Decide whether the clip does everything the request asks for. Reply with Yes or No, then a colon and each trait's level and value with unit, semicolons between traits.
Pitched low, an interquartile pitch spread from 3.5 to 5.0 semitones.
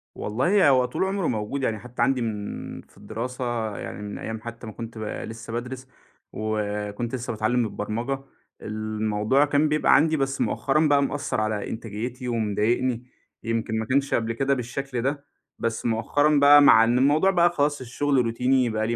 Yes: low, 120 Hz; average, 3.9 semitones